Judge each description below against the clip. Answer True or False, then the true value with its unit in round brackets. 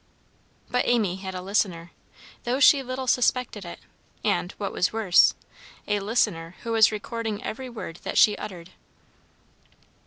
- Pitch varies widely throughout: False (4.8 semitones)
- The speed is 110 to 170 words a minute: True (145 wpm)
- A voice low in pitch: False (210 Hz)